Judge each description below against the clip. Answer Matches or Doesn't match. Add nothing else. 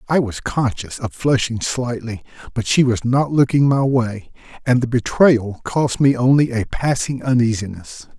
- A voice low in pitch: Matches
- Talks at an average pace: Matches